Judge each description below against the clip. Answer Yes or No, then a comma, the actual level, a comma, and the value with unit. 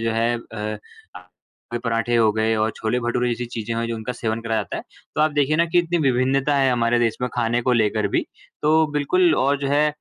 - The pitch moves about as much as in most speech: Yes, average, 3.7 semitones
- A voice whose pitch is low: Yes, low, 120 Hz